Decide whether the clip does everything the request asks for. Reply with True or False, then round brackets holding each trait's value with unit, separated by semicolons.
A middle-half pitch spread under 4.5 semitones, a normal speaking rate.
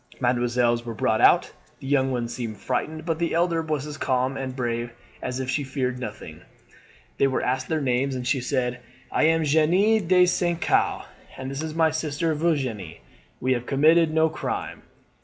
True (4.1 semitones; 185 wpm)